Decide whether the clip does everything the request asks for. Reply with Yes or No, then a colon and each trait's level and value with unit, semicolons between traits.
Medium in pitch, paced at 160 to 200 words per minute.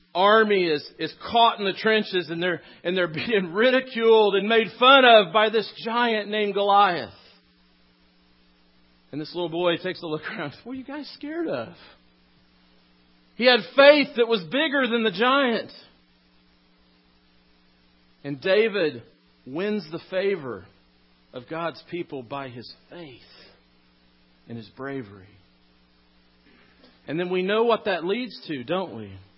No: medium, 165 Hz; average, 140 wpm